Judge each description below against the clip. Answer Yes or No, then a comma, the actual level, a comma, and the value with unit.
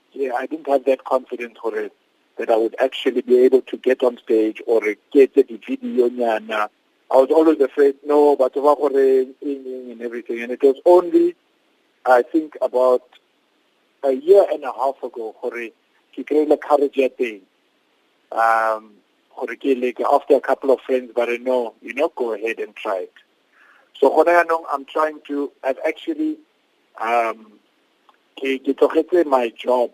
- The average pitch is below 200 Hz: Yes, medium, 140 Hz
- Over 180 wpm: No, average, 145 wpm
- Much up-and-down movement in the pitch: Yes, wide, 7.9 semitones